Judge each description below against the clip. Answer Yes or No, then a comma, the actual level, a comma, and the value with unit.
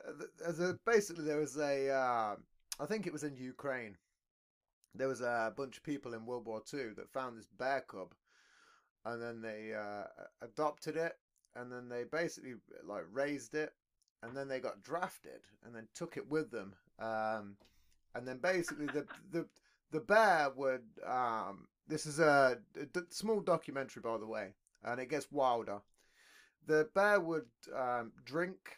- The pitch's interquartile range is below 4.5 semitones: No, average, 5.0 semitones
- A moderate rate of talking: Yes, average, 165 wpm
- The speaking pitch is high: No, medium, 140 Hz